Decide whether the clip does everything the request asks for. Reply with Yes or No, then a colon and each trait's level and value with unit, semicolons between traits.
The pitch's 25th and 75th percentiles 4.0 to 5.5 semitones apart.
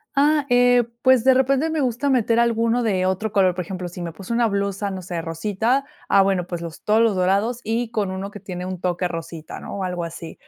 Yes: average, 4.7 semitones